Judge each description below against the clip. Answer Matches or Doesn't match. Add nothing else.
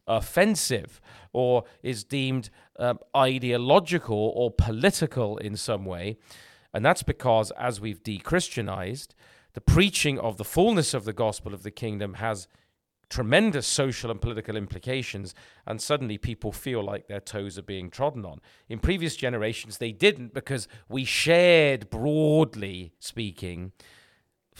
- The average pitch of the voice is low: Matches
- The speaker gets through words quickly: Doesn't match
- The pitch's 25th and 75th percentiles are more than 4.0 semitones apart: Matches